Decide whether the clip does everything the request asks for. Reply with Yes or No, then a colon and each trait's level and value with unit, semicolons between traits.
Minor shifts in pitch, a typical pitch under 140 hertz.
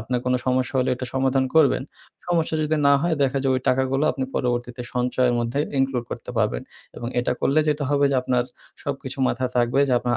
Yes: narrow, 2.0 semitones; low, 130 Hz